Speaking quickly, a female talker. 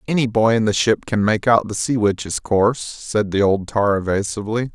No: fast, 215 wpm; male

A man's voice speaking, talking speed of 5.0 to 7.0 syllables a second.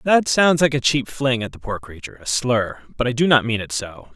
Yes: male; 5.4 syllables/s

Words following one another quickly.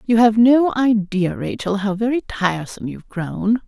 No: average, 165 wpm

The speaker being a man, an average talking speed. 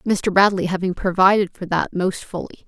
No: female; average, 180 wpm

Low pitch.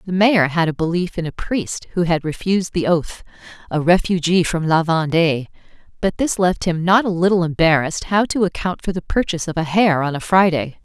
No: medium, 175 Hz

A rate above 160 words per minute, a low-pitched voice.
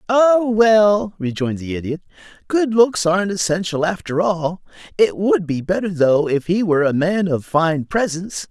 No: average, 170 wpm; medium, 185 Hz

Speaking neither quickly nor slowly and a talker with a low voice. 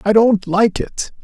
No: average, 195 wpm; high, 205 Hz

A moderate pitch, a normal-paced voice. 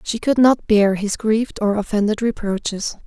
No: high, 215 Hz; average, 175 wpm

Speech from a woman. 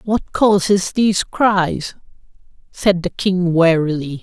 Yes: female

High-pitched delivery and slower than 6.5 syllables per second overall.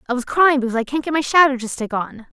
No: very high, 265 Hz; 7.0 syllables/s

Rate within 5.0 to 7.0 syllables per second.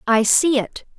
No: 4.0 syllables/s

